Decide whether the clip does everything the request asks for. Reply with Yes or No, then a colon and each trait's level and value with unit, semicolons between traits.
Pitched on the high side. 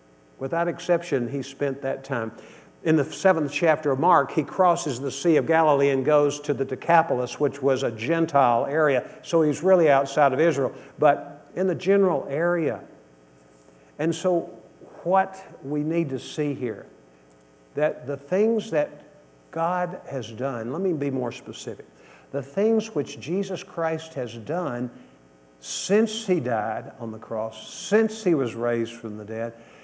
No: medium, 140 Hz